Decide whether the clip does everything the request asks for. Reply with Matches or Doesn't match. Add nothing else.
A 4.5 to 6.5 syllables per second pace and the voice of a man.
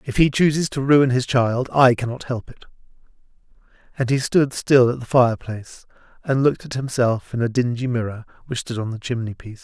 Matches